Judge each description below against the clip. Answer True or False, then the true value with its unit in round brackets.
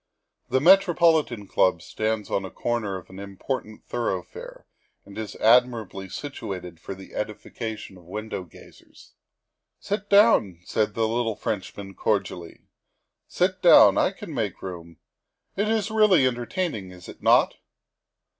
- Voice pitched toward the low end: True (110 Hz)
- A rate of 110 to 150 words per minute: True (140 wpm)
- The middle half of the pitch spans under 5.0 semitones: False (5.4 semitones)